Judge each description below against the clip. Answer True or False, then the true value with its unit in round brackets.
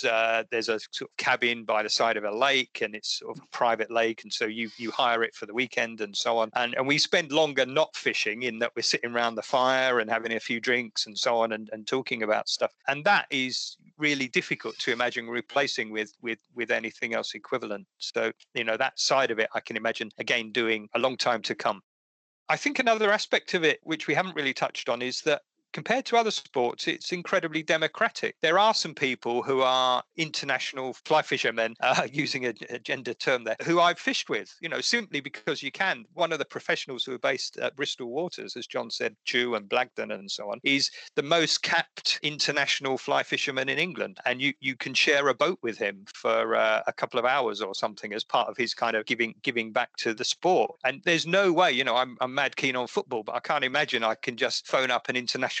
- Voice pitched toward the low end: True (130 Hz)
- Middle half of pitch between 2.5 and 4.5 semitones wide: False (5.3 semitones)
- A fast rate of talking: True (230 wpm)